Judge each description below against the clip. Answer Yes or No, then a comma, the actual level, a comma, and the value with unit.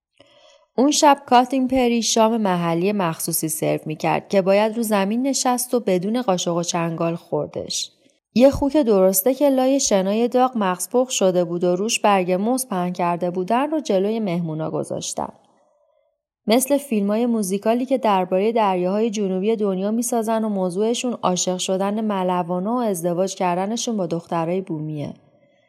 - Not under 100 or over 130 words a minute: No, average, 145 wpm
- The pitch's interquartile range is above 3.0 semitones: Yes, average, 5.1 semitones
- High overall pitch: Yes, high, 205 Hz